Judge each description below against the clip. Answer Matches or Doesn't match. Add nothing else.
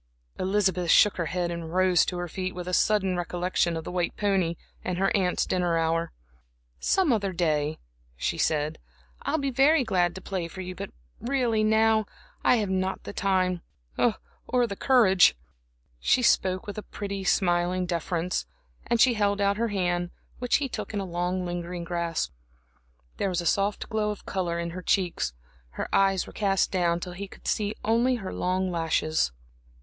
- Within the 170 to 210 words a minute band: Matches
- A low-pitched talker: Doesn't match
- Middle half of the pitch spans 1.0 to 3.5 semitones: Matches